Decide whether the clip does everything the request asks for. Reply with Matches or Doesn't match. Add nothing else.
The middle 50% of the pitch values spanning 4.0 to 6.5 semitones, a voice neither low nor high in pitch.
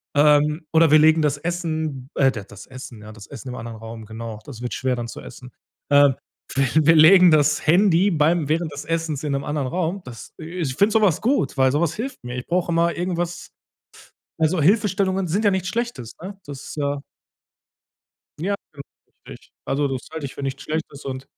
Matches